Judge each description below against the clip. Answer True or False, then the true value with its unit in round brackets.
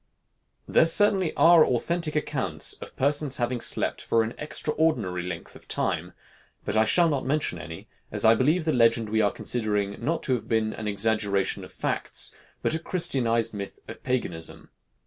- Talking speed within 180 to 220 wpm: False (170 wpm)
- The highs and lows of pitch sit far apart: True (6.2 semitones)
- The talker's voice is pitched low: True (120 Hz)